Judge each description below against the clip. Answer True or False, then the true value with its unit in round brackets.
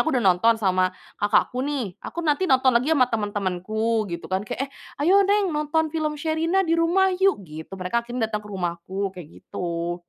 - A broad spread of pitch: True (9.0 semitones)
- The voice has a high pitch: True (230 Hz)